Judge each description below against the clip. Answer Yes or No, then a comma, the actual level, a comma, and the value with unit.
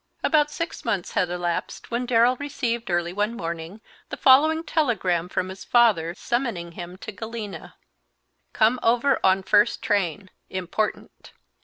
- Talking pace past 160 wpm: No, average, 140 wpm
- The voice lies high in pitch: Yes, high, 215 Hz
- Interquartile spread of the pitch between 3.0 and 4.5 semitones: No, average, 5.1 semitones